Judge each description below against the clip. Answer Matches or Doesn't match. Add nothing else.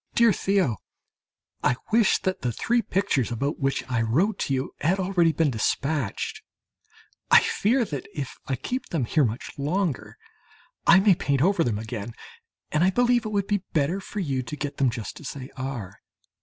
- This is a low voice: Doesn't match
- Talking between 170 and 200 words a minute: Matches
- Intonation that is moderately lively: Doesn't match